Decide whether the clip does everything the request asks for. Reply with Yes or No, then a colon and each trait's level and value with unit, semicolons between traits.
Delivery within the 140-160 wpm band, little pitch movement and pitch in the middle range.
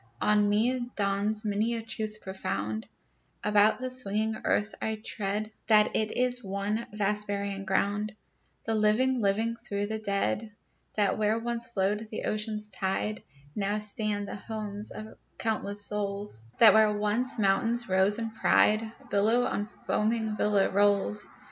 No: average, 145 wpm; narrow, 1.5 semitones; high, 210 Hz